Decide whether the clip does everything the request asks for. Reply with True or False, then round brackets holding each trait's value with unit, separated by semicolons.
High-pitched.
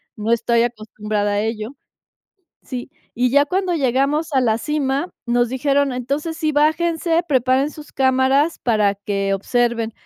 True (260 Hz)